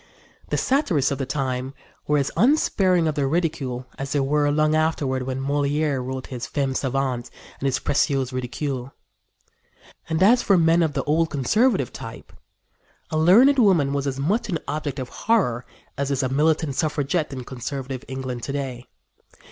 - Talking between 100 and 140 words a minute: No, average, 170 wpm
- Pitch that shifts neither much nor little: Yes, average, 3.3 semitones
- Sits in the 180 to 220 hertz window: No, medium, 140 Hz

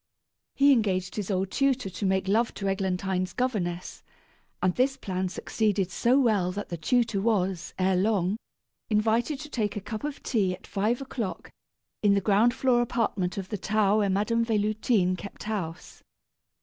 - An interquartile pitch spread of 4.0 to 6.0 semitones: No, average, 3.5 semitones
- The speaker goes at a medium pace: Yes, average, 165 wpm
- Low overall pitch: No, high, 205 Hz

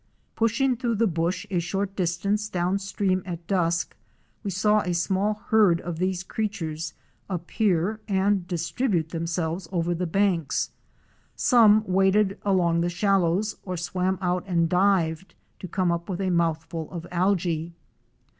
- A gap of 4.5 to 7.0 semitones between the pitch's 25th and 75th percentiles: No, average, 2.9 semitones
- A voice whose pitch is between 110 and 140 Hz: No, medium, 185 Hz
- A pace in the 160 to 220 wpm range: No, average, 140 wpm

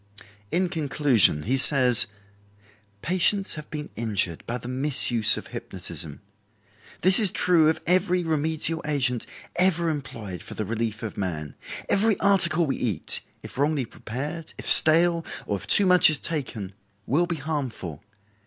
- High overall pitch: No, medium, 150 Hz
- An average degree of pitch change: No, wide, 6.6 semitones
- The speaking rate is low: No, average, 145 wpm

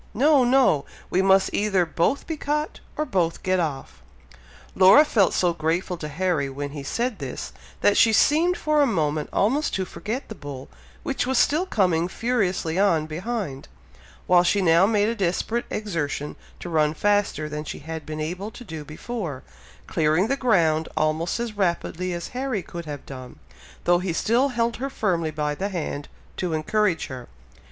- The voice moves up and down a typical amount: No, wide, 6.3 semitones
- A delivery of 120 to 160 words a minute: No, average, 175 wpm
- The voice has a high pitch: No, medium, 180 Hz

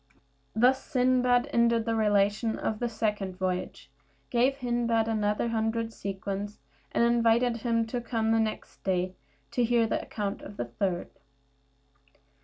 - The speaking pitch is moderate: No, high, 225 Hz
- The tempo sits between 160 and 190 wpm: No, average, 140 wpm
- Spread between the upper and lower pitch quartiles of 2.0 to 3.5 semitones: Yes, narrow, 2.4 semitones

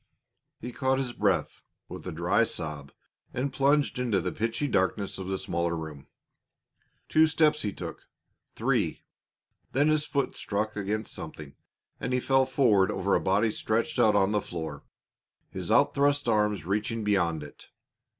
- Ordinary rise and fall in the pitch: No, wide, 6.0 semitones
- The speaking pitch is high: No, low, 105 Hz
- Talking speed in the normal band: Yes, average, 160 wpm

